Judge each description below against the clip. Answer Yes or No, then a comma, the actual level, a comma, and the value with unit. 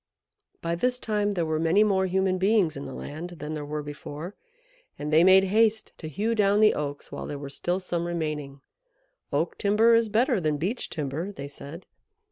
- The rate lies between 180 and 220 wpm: Yes, average, 195 wpm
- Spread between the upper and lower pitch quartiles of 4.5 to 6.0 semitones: Yes, wide, 5.4 semitones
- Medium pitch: Yes, medium, 175 Hz